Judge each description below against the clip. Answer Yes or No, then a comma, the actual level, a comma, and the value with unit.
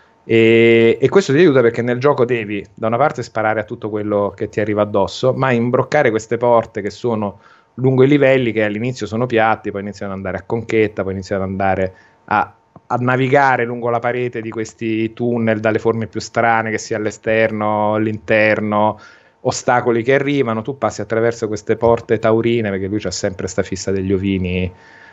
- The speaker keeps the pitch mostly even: Yes, narrow, 2.2 semitones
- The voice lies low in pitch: Yes, low, 110 Hz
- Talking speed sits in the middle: No, fast, 185 wpm